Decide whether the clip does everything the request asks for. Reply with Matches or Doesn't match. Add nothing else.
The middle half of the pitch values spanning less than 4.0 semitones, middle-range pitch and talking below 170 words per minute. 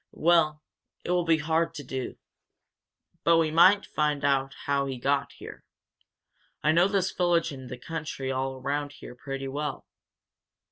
Matches